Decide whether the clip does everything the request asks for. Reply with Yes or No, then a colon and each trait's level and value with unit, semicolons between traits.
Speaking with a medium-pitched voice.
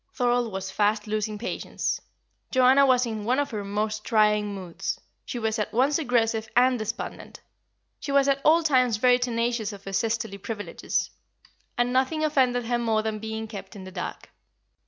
No: high, 225 Hz